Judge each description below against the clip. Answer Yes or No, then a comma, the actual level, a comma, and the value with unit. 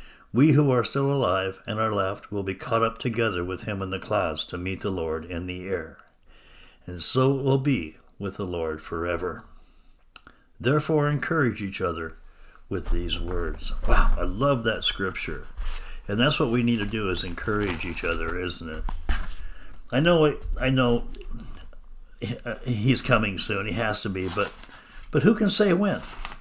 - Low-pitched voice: Yes, low, 100 Hz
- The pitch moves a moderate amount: No, wide, 6.4 semitones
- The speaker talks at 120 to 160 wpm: No, average, 175 wpm